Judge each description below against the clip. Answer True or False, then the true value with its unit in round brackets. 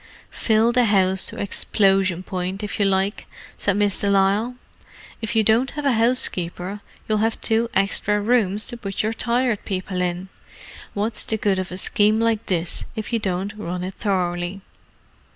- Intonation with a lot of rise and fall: False (2.8 semitones)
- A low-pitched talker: False (205 Hz)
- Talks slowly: False (170 wpm)